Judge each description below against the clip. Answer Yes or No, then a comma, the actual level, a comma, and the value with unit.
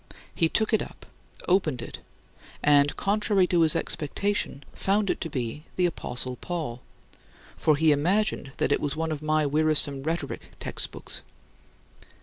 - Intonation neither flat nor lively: Yes, average, 4.0 semitones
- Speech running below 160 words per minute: Yes, average, 145 wpm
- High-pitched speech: No, medium, 155 Hz